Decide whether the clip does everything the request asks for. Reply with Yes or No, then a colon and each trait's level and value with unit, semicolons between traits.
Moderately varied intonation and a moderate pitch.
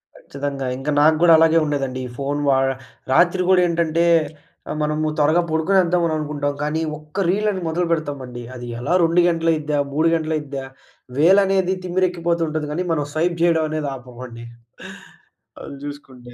Yes: average, 3.0 semitones; medium, 155 Hz